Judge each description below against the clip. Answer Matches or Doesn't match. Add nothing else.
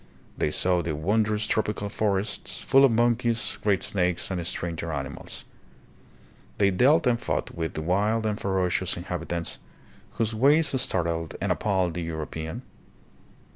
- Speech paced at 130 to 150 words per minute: Matches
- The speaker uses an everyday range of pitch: Matches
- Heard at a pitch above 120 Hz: Doesn't match